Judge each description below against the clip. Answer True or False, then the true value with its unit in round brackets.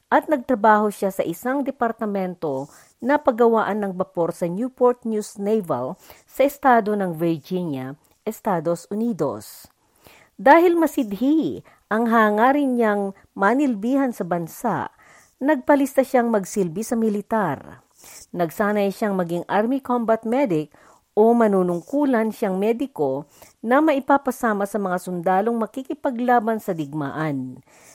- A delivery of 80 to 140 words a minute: True (110 wpm)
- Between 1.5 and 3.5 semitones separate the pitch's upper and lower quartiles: False (5.3 semitones)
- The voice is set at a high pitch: True (220 Hz)